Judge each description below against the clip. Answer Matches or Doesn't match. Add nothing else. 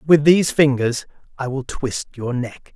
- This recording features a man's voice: Matches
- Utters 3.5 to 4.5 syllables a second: Matches